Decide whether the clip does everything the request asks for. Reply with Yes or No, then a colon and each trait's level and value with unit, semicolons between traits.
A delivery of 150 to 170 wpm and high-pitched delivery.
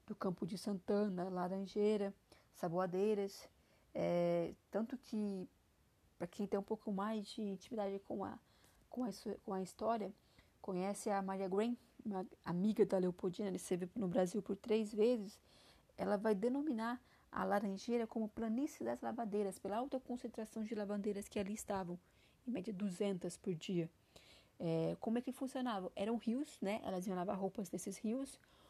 Yes: average, 155 wpm; high, 205 Hz